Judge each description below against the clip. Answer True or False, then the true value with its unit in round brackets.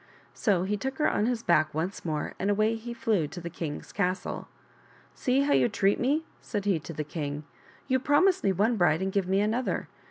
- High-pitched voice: True (200 Hz)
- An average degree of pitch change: False (5.7 semitones)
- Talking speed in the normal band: False (225 wpm)